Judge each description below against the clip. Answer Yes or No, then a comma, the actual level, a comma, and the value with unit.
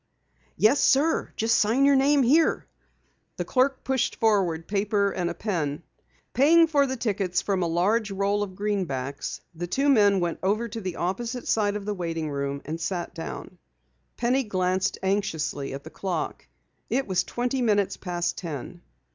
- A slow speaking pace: No, average, 165 wpm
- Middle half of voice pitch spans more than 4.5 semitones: Yes, average, 5.3 semitones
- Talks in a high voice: Yes, high, 200 Hz